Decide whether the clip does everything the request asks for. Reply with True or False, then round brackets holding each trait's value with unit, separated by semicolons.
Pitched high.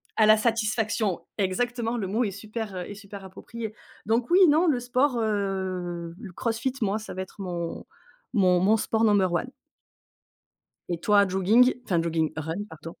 True (205 Hz)